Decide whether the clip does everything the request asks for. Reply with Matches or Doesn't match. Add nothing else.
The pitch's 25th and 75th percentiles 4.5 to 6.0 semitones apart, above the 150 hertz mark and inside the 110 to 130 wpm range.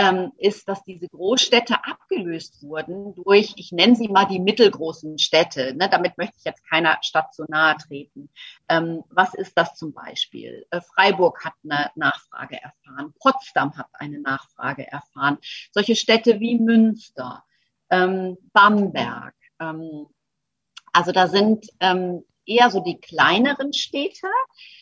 Matches